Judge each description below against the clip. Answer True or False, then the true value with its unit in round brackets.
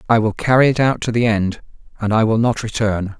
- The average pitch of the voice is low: True (110 Hz)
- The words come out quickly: True (245 wpm)